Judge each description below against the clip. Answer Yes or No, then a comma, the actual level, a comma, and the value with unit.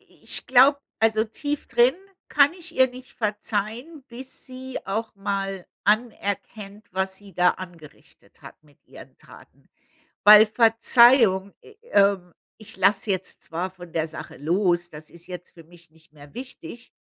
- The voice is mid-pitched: No, high, 205 Hz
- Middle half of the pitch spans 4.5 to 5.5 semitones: Yes, average, 5.2 semitones